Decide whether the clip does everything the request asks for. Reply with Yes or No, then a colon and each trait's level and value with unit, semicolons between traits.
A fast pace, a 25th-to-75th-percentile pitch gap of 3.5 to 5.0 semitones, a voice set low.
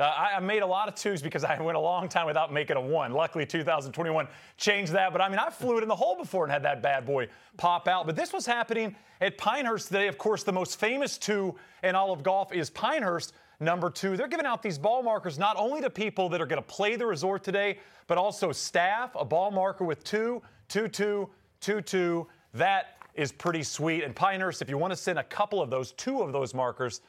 No: fast, 240 wpm; average, 4.1 semitones; high, 190 Hz